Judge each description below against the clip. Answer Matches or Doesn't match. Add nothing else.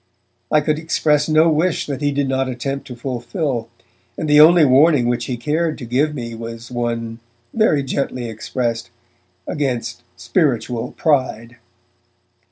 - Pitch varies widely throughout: Doesn't match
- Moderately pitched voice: Doesn't match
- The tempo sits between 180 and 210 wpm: Doesn't match